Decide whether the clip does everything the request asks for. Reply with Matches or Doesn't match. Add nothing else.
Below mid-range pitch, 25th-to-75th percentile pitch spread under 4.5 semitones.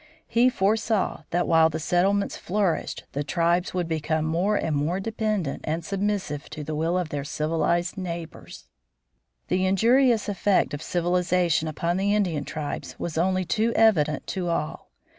Doesn't match